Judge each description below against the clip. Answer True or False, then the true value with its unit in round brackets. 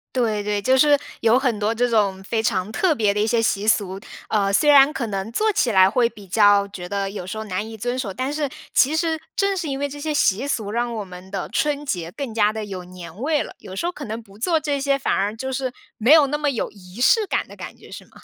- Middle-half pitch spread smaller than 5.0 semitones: False (5.6 semitones)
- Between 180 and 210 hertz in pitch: False (225 Hz)